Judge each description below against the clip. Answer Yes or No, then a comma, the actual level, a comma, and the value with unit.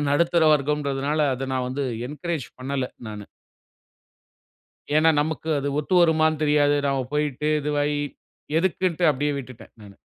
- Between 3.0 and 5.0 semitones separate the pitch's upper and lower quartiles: No, narrow, 2.5 semitones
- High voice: No, medium, 145 Hz